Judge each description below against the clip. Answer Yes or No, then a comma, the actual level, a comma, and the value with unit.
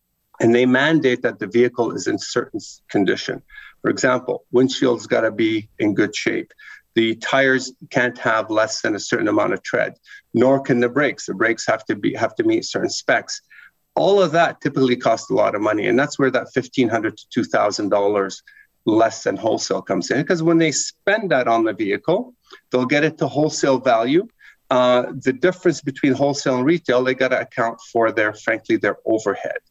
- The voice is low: Yes, low, 130 Hz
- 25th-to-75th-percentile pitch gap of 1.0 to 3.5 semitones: No, average, 5.1 semitones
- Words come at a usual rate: Yes, average, 195 wpm